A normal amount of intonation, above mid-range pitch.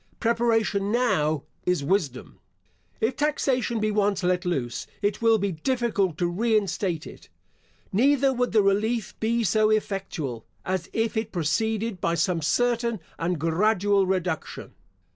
Yes: average, 4.3 semitones; high, 205 Hz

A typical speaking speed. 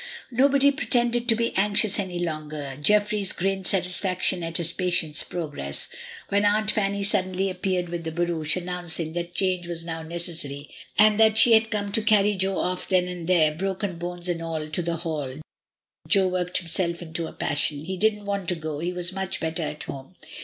Yes: average, 190 wpm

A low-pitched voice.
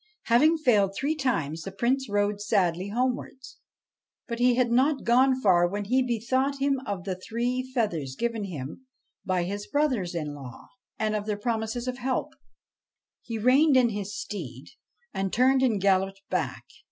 No: high, 220 Hz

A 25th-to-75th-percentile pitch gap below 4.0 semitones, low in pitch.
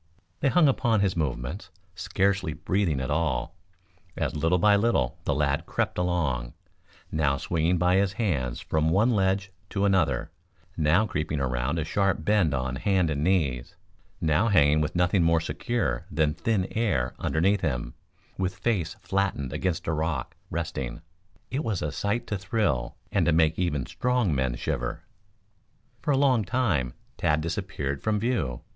No: average, 5.2 semitones; very low, 85 Hz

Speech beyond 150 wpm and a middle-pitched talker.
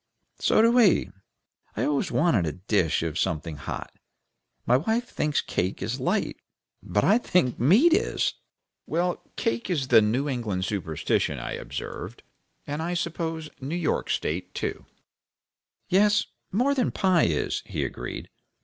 No: average, 140 wpm; medium, 145 Hz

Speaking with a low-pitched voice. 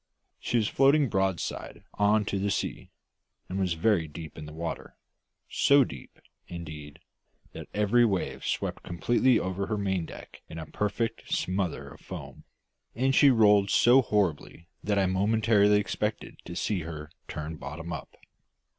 Yes: low, 100 Hz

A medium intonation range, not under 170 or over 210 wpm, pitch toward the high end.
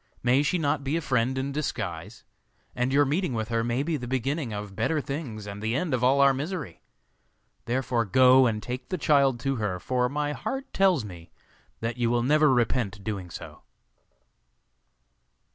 No: average, 3.9 semitones; average, 180 wpm; low, 130 Hz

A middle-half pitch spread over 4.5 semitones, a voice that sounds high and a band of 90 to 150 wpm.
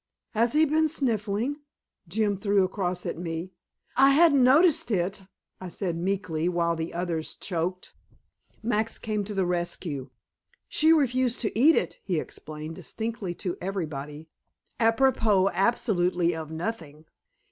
Yes: average, 5.1 semitones; high, 195 Hz; slow, 135 wpm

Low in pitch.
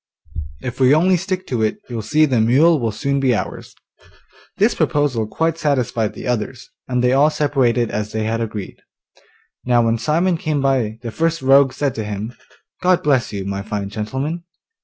Yes: low, 125 Hz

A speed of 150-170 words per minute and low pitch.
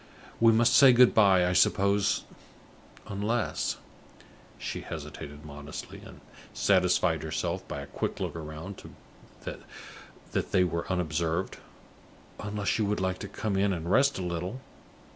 No: slow, 135 wpm; very low, 95 Hz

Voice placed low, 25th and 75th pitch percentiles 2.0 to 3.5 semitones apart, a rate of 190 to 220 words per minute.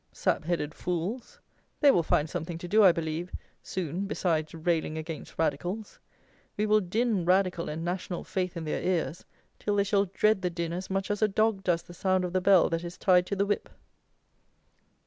No: medium, 180 Hz; average, 2.9 semitones; average, 195 wpm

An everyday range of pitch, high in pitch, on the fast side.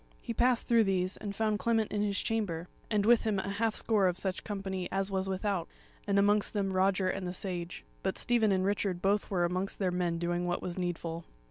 No: narrow, 2.3 semitones; high, 195 Hz; fast, 220 wpm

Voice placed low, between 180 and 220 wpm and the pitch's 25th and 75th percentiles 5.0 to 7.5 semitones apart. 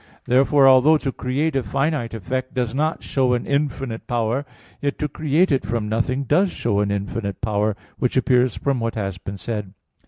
No: low, 125 Hz; average, 195 wpm; average, 4.1 semitones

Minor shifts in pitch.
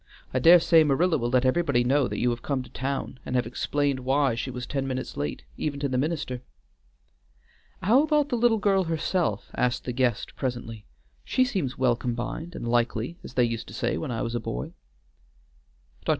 No: average, 5.0 semitones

